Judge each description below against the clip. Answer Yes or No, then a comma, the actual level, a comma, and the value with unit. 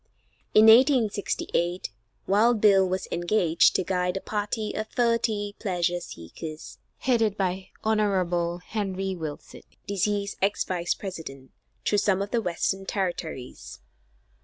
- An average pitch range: Yes, average, 3.2 semitones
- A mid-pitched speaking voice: No, high, 195 Hz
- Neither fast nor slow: No, slow, 120 wpm